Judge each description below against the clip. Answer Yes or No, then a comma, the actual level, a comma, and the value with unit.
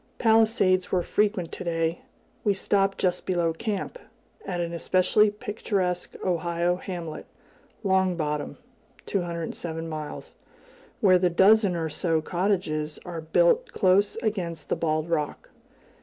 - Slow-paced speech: Yes, slow, 125 wpm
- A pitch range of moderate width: Yes, average, 3.0 semitones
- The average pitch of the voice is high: No, medium, 180 Hz